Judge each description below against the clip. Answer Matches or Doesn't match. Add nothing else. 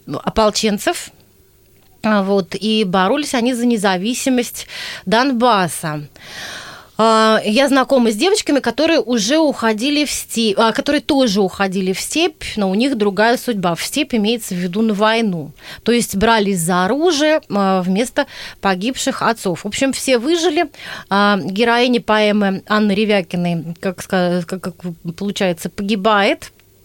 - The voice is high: Matches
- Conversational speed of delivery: Matches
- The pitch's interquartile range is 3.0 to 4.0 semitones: Doesn't match